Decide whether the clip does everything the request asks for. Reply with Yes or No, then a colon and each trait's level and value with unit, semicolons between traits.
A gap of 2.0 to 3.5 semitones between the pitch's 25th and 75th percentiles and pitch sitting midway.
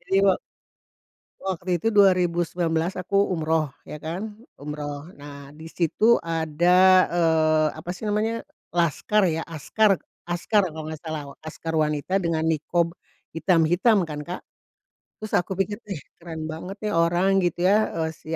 Yes: average, 3.0 semitones; medium, 170 Hz